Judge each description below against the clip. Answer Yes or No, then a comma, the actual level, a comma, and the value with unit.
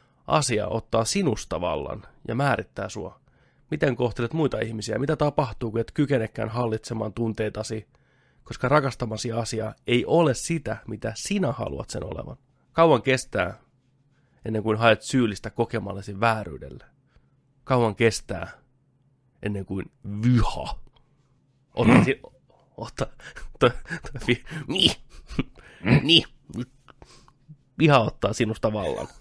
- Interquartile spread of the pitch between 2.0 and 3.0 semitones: No, average, 3.7 semitones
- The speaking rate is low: Yes, slow, 90 wpm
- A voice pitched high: No, low, 120 Hz